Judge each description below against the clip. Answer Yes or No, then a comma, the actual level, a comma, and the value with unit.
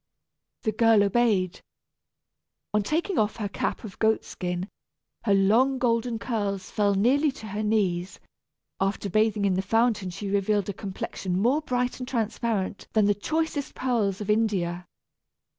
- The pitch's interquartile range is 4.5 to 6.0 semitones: No, average, 3.0 semitones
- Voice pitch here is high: Yes, high, 210 Hz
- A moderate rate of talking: Yes, average, 150 wpm